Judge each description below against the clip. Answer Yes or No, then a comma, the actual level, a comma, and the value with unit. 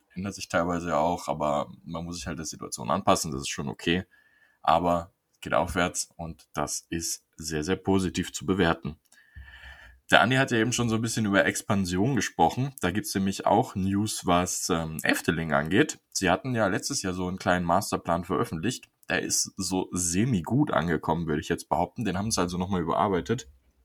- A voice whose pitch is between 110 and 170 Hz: No, very low, 90 Hz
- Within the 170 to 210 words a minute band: Yes, fast, 190 wpm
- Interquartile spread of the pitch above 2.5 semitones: Yes, average, 2.9 semitones